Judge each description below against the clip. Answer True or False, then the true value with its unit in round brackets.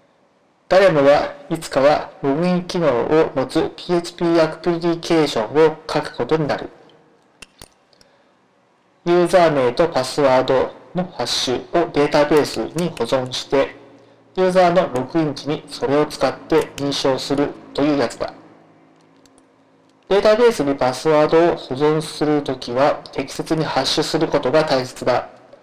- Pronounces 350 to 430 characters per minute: False (295 characters per minute)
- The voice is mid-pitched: True (150 Hz)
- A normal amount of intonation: True (3.6 semitones)